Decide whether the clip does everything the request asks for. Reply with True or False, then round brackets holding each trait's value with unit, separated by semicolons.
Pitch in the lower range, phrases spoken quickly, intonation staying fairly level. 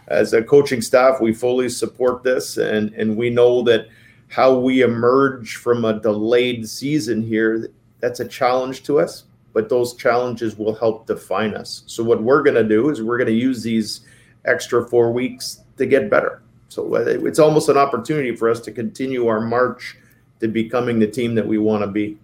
False (120 Hz; 190 wpm; 2.3 semitones)